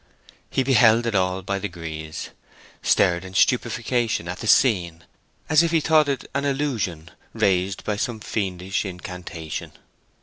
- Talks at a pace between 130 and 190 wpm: Yes, average, 140 wpm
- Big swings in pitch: Yes, wide, 5.7 semitones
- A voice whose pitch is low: Yes, low, 100 Hz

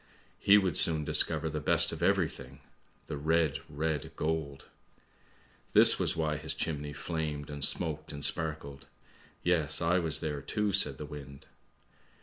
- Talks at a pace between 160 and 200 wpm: No, average, 150 wpm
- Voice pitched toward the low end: Yes, very low, 75 Hz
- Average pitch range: No, narrow, 1.9 semitones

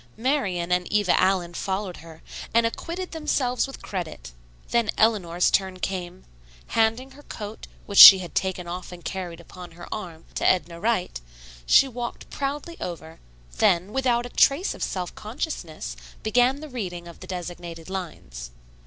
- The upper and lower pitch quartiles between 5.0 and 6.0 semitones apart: Yes, wide, 5.5 semitones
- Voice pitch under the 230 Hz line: Yes, high, 190 Hz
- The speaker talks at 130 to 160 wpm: Yes, average, 155 wpm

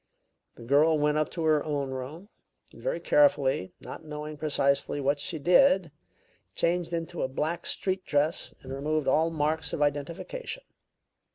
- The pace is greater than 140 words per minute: Yes, average, 155 wpm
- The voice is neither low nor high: Yes, medium, 155 Hz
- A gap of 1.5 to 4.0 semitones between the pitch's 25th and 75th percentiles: Yes, average, 2.8 semitones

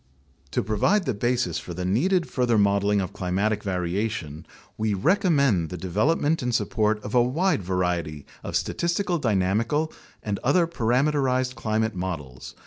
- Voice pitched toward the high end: No, low, 110 Hz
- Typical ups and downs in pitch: No, wide, 6.5 semitones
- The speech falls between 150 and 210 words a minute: No, average, 140 wpm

